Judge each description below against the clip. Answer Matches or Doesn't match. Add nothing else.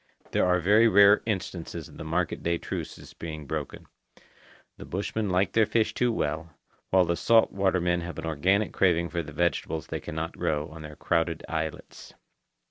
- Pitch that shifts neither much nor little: Matches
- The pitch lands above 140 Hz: Doesn't match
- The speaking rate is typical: Matches